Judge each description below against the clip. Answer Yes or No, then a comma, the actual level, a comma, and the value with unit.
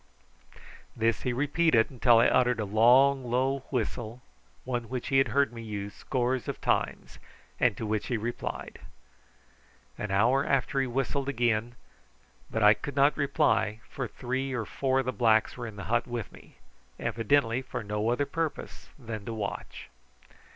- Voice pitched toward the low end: Yes, low, 120 Hz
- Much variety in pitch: No, average, 3.1 semitones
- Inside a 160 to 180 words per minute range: Yes, average, 165 wpm